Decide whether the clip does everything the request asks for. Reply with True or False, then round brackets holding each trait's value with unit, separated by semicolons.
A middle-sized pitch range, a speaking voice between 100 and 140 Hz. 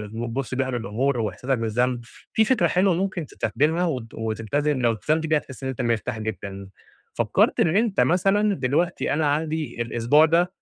False (5.8 semitones; 135 Hz)